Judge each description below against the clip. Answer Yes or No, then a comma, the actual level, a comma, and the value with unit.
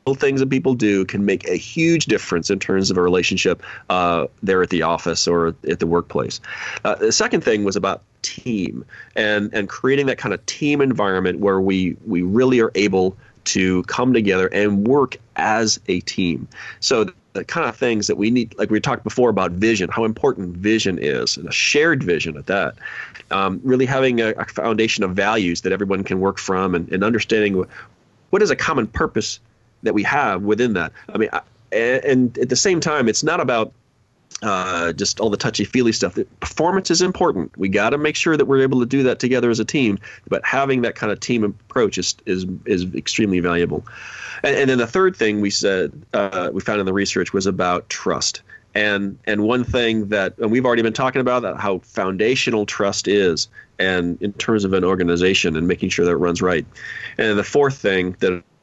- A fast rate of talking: Yes, fast, 210 wpm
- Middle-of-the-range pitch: No, low, 105 Hz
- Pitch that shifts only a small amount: No, average, 4.6 semitones